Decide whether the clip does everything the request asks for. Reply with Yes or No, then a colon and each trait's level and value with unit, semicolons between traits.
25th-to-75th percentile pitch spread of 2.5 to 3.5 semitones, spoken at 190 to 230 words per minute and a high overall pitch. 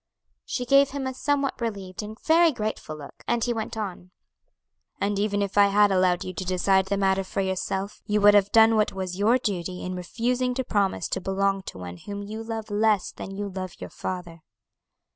Yes: average, 2.9 semitones; fast, 205 wpm; high, 200 Hz